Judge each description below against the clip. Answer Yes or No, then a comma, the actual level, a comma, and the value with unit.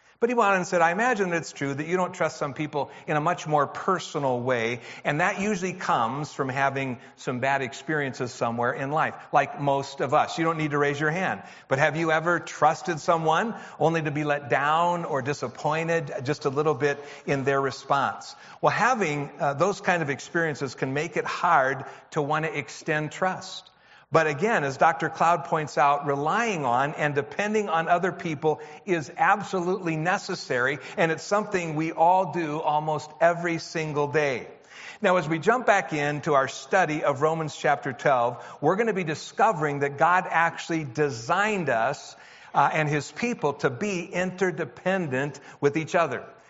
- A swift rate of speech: Yes, fast, 180 wpm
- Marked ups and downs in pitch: No, average, 3.5 semitones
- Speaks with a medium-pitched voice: Yes, medium, 155 Hz